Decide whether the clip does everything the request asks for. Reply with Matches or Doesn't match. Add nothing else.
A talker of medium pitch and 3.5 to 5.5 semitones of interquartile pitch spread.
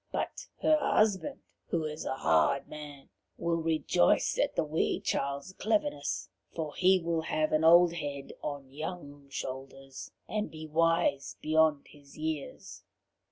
Doesn't match